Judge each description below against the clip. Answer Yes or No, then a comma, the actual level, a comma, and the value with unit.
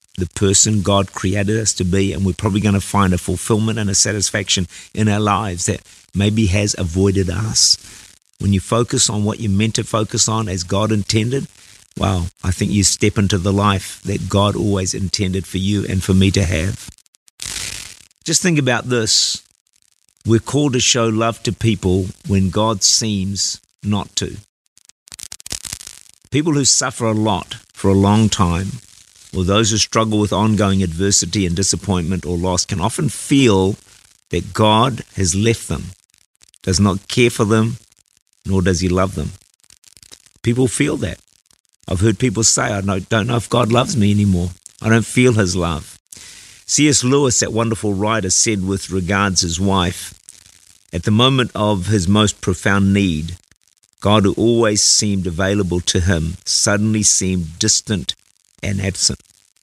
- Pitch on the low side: Yes, low, 100 Hz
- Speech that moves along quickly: No, average, 165 wpm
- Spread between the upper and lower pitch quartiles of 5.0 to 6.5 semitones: No, average, 2.7 semitones